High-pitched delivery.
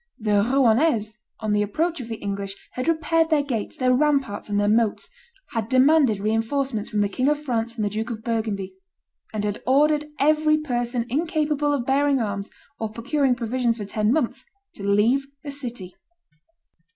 Yes: high, 240 Hz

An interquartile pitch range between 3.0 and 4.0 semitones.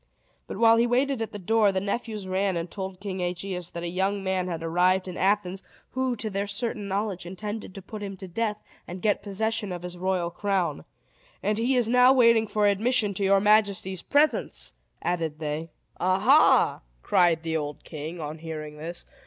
Yes: average, 3.3 semitones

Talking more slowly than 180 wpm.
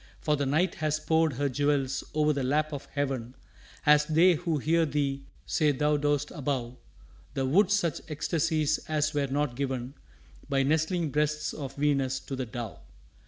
Yes: average, 165 wpm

